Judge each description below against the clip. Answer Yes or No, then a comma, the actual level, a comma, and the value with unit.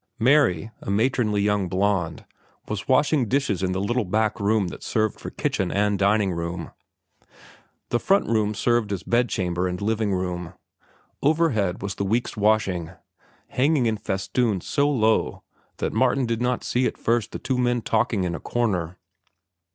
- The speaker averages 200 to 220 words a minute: No, average, 160 wpm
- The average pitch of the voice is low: Yes, low, 105 Hz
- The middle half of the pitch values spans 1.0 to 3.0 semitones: No, average, 4.2 semitones